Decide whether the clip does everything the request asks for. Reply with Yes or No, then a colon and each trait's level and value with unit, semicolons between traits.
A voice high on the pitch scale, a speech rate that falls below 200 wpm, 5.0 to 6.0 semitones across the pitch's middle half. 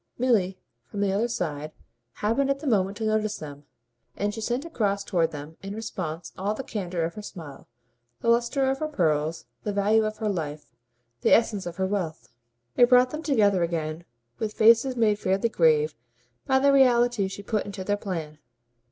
Yes: high, 205 Hz; average, 185 wpm; wide, 5.4 semitones